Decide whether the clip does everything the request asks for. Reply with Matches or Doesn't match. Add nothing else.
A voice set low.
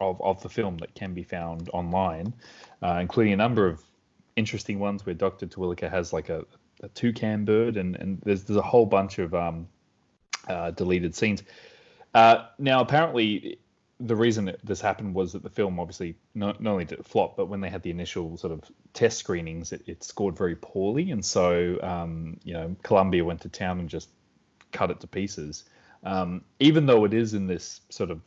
Matches